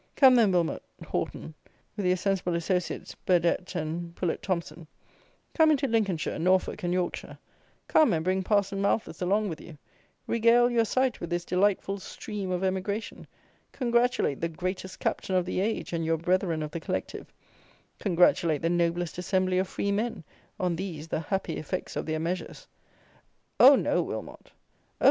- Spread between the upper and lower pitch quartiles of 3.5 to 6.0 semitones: No, average, 3.0 semitones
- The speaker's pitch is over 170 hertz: Yes, medium, 185 Hz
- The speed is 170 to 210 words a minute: No, average, 160 wpm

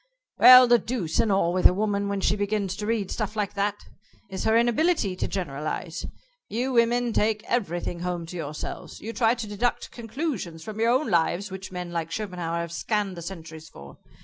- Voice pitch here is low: No, high, 200 Hz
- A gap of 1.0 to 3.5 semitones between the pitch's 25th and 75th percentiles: No, average, 4.6 semitones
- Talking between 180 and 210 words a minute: Yes, average, 195 wpm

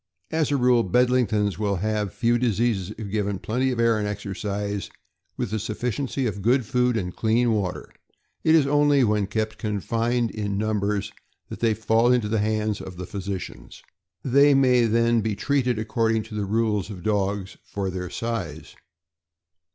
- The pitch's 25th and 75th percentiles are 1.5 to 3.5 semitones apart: Yes, average, 2.8 semitones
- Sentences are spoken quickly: No, average, 170 wpm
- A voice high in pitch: No, low, 110 Hz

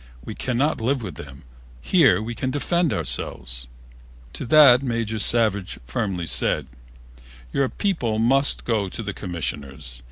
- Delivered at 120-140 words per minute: Yes, slow, 135 wpm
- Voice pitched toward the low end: Yes, low, 115 Hz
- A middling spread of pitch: No, wide, 6.7 semitones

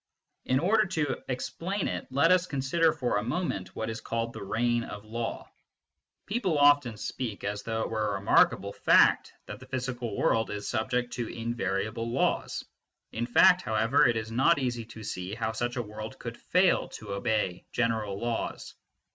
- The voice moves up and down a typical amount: Yes, average, 3.5 semitones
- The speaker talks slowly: No, average, 170 wpm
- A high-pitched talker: No, low, 120 Hz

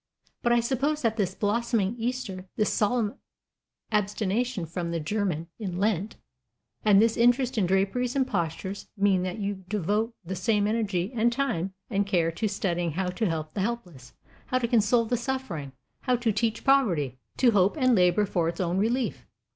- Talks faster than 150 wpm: Yes, average, 175 wpm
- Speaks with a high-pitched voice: Yes, high, 205 Hz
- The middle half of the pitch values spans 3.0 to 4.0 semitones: No, average, 4.5 semitones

